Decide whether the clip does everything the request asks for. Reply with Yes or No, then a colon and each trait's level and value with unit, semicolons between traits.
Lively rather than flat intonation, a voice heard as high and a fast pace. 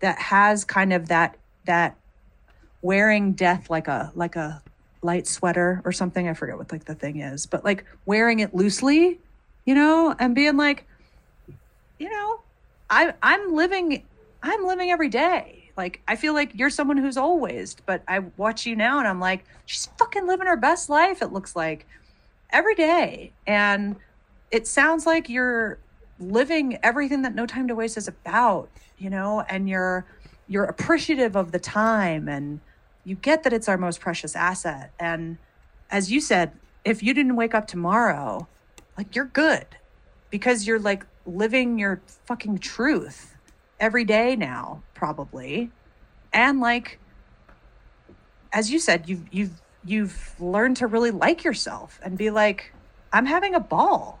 No: wide, 6.9 semitones; high, 215 Hz; average, 160 wpm